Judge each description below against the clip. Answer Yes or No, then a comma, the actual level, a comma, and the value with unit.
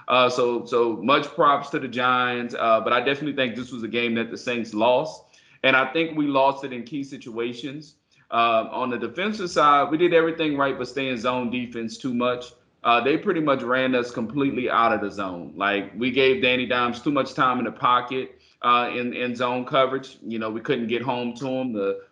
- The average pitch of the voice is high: No, low, 125 Hz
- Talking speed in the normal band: No, fast, 220 wpm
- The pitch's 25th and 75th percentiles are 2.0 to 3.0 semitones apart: Yes, narrow, 2.5 semitones